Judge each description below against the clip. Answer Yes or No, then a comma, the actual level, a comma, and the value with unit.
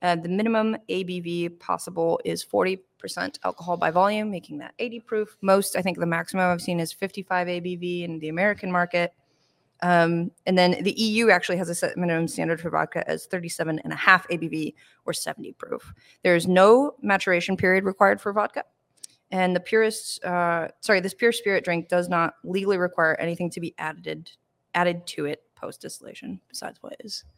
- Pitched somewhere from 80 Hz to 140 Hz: No, medium, 180 Hz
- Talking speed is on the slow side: No, average, 175 wpm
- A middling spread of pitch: No, narrow, 2.3 semitones